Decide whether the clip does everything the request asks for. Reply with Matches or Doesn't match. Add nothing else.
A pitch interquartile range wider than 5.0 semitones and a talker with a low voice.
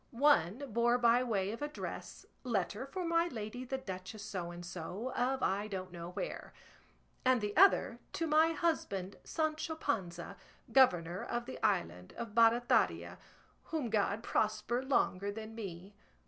Doesn't match